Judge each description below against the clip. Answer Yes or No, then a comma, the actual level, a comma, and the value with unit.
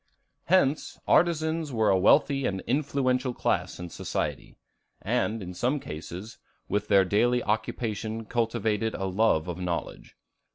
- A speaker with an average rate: No, slow, 130 wpm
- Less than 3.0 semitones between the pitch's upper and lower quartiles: No, average, 4.8 semitones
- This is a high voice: No, low, 110 Hz